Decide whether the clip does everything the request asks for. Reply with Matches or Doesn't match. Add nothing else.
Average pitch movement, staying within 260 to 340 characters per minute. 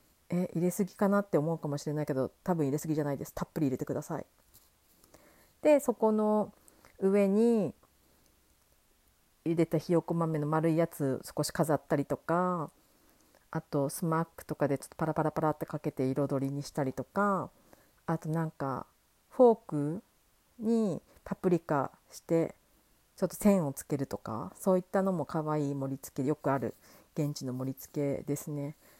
Matches